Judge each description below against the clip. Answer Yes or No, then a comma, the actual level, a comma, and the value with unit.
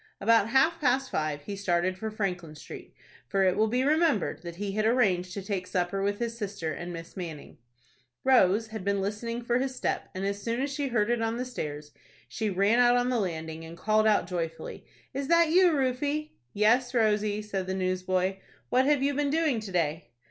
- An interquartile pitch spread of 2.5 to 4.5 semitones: No, average, 5.2 semitones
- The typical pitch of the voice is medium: No, high, 210 Hz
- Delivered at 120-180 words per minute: No, fast, 205 wpm